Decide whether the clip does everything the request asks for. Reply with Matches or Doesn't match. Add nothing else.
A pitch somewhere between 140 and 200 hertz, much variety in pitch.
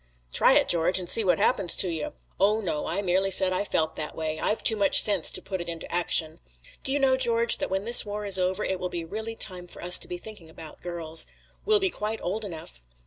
Doesn't match